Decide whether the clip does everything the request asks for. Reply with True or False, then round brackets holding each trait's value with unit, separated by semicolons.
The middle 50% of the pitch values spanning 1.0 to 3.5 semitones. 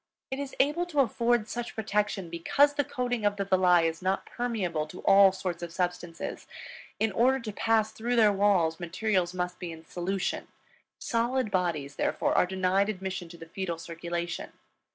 False (4.6 semitones)